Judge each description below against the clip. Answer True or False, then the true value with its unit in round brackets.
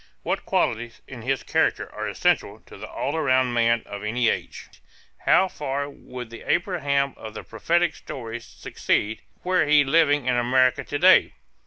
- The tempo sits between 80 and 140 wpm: False (165 wpm)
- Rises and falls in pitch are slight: False (3.9 semitones)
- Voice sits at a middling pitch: False (130 Hz)